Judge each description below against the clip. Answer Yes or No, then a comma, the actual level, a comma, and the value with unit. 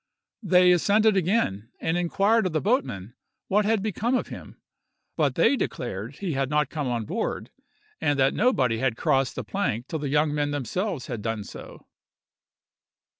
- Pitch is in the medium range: Yes, medium, 150 Hz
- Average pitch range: No, wide, 7.6 semitones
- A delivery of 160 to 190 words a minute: Yes, average, 170 wpm